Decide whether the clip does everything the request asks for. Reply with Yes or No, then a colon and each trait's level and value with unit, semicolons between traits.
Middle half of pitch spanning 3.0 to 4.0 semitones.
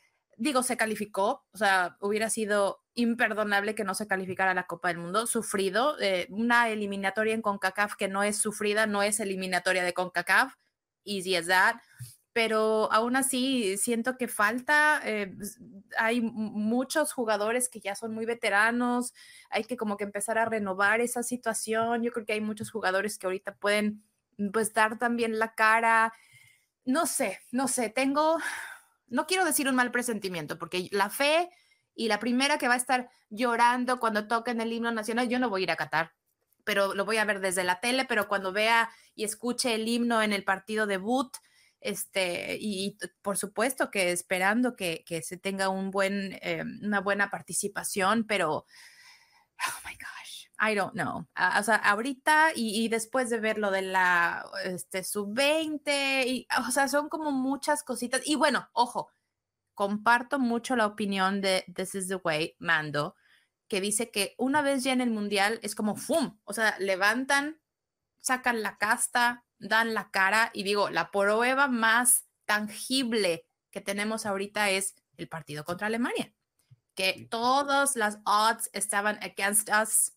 Yes: average, 3.6 semitones